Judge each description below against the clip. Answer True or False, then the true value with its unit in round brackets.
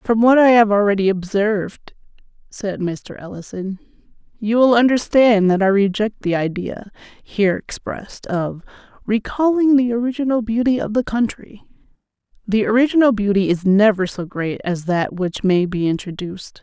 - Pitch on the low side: False (210 Hz)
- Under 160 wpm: True (145 wpm)